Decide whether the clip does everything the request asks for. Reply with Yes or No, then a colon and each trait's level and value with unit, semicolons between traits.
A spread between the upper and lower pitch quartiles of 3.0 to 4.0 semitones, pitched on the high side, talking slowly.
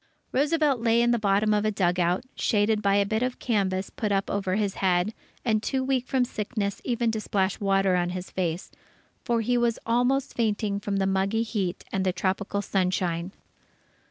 No: average, 3.4 semitones; high, 205 Hz; average, 185 wpm